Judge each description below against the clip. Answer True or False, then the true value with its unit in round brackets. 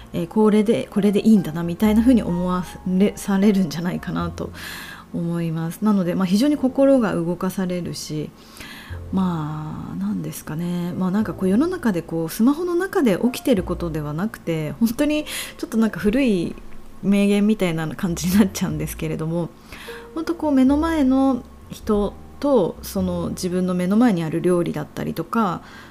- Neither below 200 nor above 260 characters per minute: False (365 characters per minute)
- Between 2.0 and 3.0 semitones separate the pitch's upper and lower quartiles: False (5.3 semitones)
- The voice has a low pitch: False (195 Hz)